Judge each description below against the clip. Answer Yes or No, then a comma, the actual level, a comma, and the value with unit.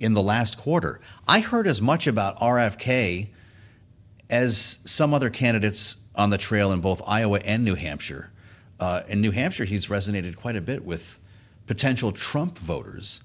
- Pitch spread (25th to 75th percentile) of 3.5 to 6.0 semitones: No, average, 3.1 semitones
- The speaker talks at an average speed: Yes, average, 165 wpm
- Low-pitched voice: Yes, low, 105 Hz